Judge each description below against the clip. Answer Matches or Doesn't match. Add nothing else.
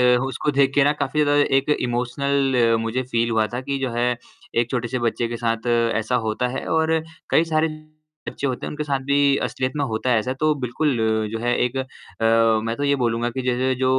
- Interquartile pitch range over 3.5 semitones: Doesn't match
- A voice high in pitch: Doesn't match